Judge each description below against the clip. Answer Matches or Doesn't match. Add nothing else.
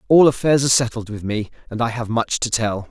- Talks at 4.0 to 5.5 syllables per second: Doesn't match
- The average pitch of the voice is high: Doesn't match